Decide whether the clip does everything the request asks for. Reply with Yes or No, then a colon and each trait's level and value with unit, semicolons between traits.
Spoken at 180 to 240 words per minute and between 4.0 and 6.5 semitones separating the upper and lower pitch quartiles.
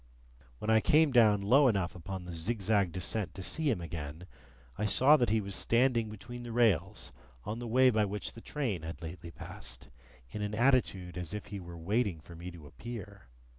Yes: average, 200 wpm; average, 5.1 semitones